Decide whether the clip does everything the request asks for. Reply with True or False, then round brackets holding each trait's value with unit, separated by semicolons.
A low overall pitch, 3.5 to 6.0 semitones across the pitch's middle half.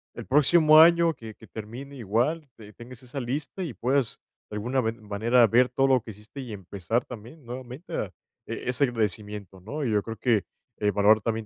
True (120 Hz; 4.1 semitones)